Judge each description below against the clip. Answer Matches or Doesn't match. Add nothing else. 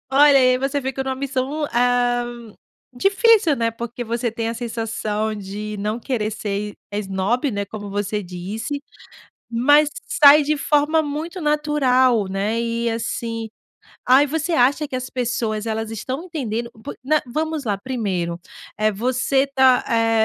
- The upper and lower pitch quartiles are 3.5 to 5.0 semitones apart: Matches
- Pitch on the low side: Doesn't match